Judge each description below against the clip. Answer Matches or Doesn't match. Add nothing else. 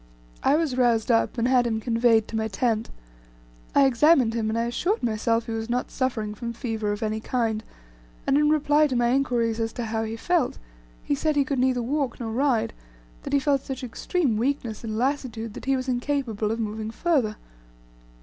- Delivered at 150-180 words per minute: Doesn't match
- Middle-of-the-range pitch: Doesn't match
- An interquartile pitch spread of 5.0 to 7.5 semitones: Doesn't match